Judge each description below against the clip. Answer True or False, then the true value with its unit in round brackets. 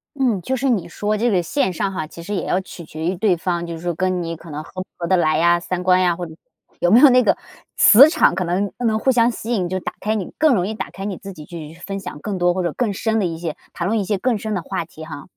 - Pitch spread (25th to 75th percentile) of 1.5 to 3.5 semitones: False (4.0 semitones)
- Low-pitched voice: False (185 Hz)